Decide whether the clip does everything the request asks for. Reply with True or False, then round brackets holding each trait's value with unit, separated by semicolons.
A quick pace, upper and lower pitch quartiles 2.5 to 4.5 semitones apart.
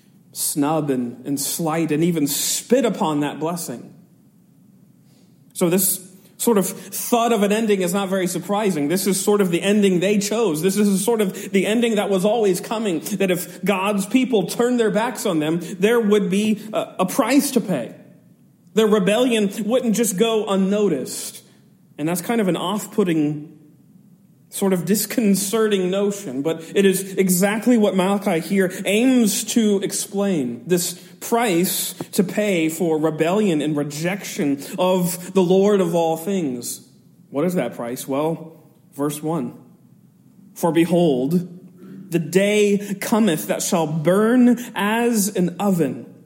False (150 wpm; 3.5 semitones)